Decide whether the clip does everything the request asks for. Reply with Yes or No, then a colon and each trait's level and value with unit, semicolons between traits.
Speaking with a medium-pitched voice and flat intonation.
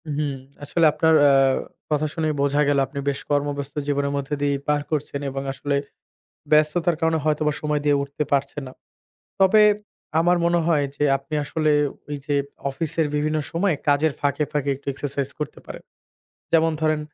Yes: medium, 150 Hz; narrow, 1.7 semitones